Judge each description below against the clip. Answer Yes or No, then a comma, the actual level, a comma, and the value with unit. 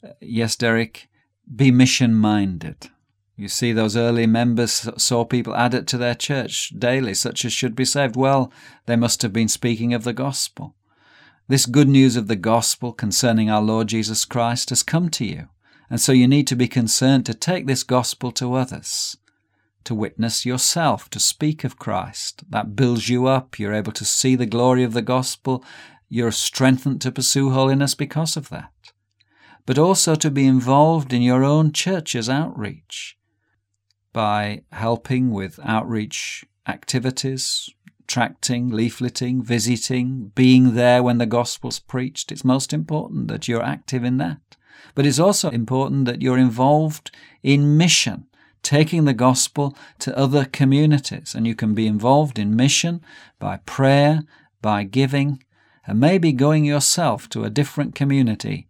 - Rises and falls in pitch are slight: No, average, 3.2 semitones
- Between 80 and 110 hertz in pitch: No, low, 125 Hz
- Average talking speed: Yes, average, 155 wpm